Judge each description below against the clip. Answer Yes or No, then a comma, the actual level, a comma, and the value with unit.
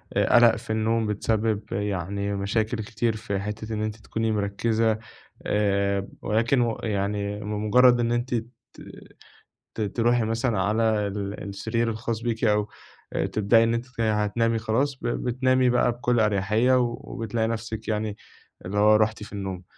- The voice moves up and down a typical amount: No, narrow, 2.1 semitones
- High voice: No, low, 110 Hz